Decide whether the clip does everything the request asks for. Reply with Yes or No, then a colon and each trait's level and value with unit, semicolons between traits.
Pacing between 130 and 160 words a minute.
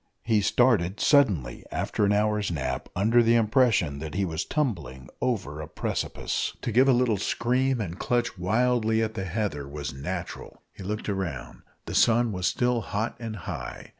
No: average, 170 wpm